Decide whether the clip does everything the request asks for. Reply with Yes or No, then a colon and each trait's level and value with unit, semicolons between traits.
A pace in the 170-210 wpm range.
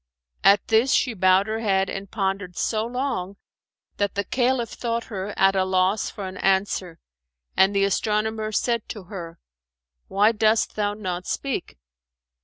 No: average, 155 wpm